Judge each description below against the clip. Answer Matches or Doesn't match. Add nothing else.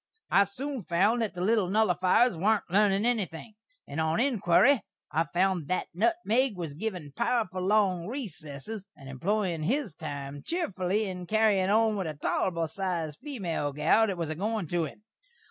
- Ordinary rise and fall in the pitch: Matches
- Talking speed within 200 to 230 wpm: Doesn't match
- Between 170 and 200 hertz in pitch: Matches